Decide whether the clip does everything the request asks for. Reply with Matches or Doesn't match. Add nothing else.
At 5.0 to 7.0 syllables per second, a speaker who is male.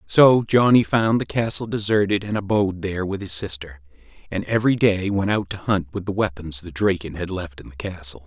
Matches